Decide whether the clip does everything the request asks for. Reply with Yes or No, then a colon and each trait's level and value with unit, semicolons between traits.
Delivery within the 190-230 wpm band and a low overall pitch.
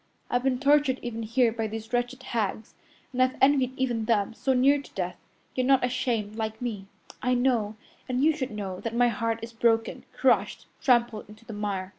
No: average, 195 wpm; high, 235 Hz